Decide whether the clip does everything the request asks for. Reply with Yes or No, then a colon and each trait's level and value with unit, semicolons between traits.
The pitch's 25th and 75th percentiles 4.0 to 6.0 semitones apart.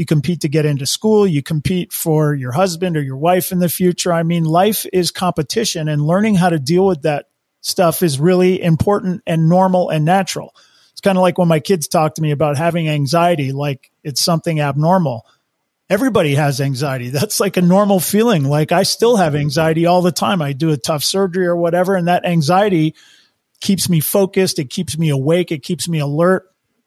No: average, 3.2 semitones